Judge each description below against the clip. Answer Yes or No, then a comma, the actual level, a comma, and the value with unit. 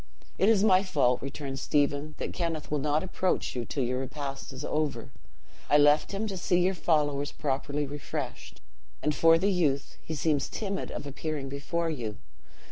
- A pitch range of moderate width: Yes, average, 3.3 semitones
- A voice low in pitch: No, medium, 150 Hz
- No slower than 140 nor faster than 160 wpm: No, average, 175 wpm